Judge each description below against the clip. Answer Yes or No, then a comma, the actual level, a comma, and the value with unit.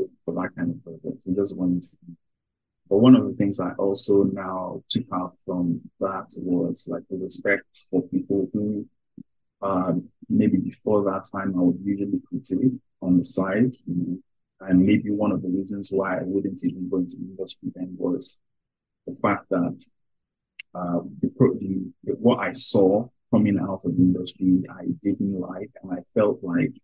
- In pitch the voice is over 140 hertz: No, very low, 95 Hz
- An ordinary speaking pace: Yes, average, 175 wpm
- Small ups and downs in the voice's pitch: Yes, narrow, 1.7 semitones